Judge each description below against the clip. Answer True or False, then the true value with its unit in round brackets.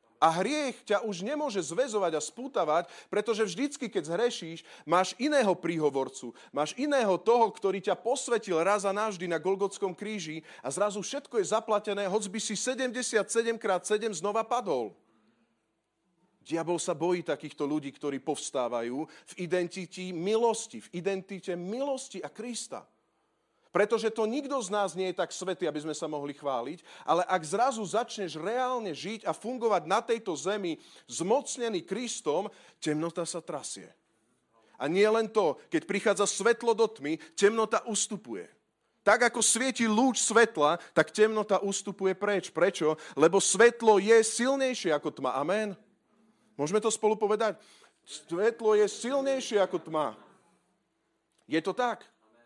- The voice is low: False (205 Hz)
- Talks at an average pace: True (145 wpm)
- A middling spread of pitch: True (4.8 semitones)